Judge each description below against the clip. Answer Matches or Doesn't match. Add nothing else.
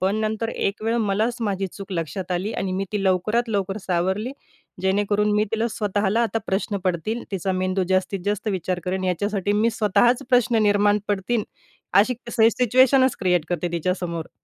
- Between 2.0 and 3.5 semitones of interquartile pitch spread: Matches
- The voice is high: Matches